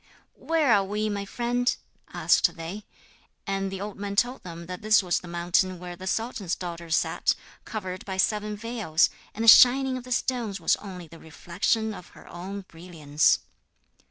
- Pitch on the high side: Yes, high, 195 Hz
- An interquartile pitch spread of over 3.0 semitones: Yes, average, 3.9 semitones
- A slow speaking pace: No, average, 175 wpm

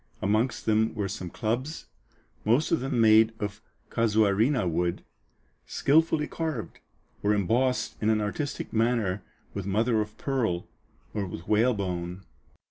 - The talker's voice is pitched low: Yes, low, 110 Hz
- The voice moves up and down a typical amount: Yes, average, 3.7 semitones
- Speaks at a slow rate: Yes, slow, 125 wpm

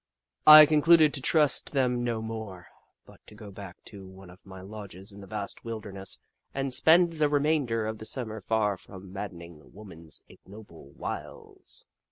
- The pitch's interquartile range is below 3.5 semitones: No, wide, 5.5 semitones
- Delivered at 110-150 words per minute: No, average, 170 wpm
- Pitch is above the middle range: No, low, 110 Hz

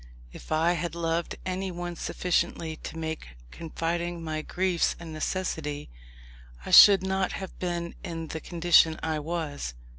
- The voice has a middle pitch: Yes, medium, 170 Hz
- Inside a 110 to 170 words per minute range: Yes, average, 140 wpm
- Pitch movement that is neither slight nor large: No, narrow, 1.7 semitones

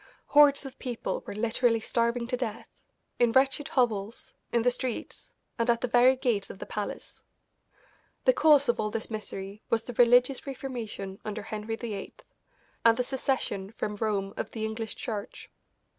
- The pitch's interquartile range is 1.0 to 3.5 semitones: Yes, average, 2.8 semitones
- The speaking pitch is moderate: No, high, 230 Hz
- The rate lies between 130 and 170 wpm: Yes, average, 165 wpm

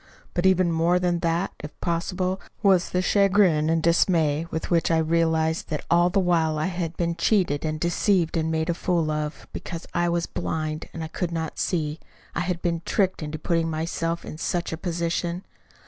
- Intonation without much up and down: Yes, narrow, 1.8 semitones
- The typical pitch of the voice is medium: Yes, medium, 170 Hz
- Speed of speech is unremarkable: Yes, average, 190 wpm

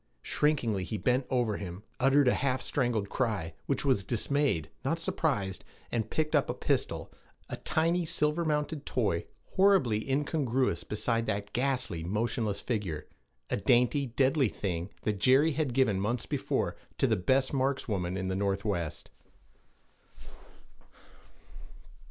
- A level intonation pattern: No, wide, 5.5 semitones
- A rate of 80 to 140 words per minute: Yes, slow, 135 wpm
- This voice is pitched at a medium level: No, low, 120 Hz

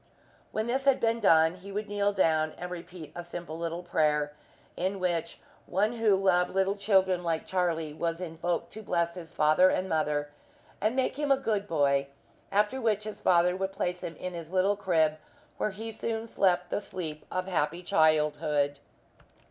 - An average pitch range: Yes, average, 3.8 semitones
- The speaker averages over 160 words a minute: Yes, average, 175 wpm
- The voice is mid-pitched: Yes, medium, 180 Hz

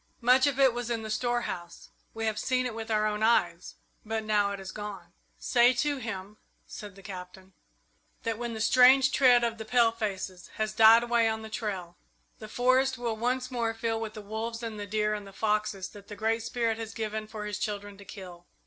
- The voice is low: No, high, 220 Hz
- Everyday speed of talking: No, fast, 210 wpm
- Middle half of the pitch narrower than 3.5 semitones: Yes, narrow, 2.4 semitones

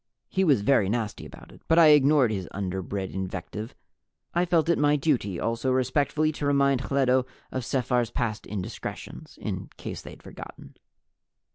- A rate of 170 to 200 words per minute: No, average, 155 wpm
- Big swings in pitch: Yes, wide, 5.7 semitones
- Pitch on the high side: No, low, 130 Hz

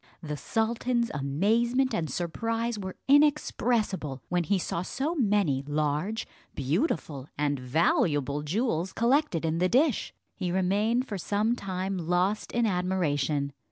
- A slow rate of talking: Yes, slow, 125 wpm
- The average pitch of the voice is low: No, high, 190 Hz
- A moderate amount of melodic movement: No, wide, 7.0 semitones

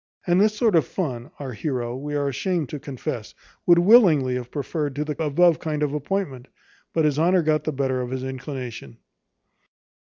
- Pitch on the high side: No, medium, 145 Hz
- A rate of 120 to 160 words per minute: No, average, 180 wpm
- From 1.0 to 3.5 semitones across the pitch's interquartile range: No, average, 4.3 semitones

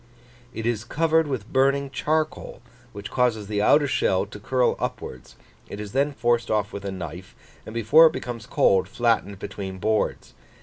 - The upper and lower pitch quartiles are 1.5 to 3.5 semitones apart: No, average, 4.8 semitones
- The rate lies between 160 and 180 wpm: Yes, average, 170 wpm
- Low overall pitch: Yes, low, 115 Hz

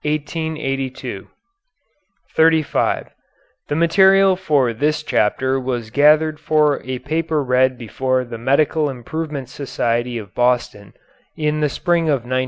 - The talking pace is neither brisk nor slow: No, slow, 125 wpm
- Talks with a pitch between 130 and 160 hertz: Yes, medium, 140 Hz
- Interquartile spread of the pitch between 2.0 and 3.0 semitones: No, average, 3.7 semitones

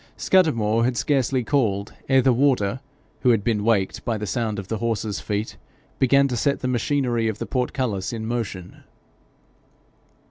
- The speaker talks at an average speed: Yes, average, 165 wpm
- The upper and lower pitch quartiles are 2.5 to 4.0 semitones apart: Yes, average, 3.6 semitones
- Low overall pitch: Yes, low, 115 Hz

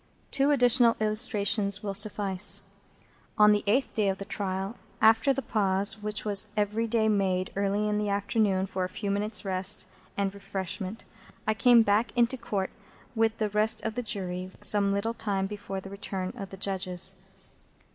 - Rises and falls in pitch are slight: Yes, narrow, 2.1 semitones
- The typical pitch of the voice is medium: No, high, 205 Hz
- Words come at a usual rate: Yes, average, 170 wpm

